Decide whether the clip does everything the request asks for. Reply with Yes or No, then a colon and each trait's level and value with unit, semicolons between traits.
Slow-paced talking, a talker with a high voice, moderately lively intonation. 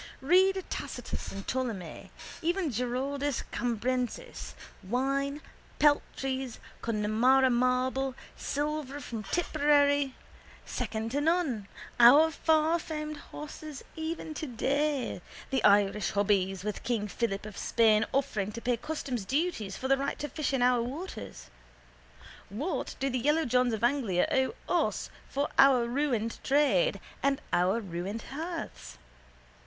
Yes: slow, 120 wpm; very high, 260 Hz; average, 4.5 semitones